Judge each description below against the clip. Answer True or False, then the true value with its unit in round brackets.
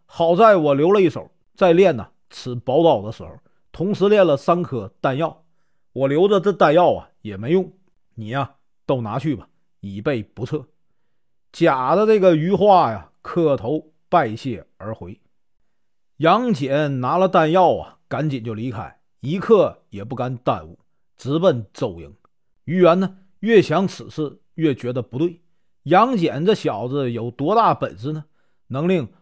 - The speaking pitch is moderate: True (145 Hz)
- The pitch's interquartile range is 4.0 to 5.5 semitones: False (6.6 semitones)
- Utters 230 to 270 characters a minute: False (215 characters per minute)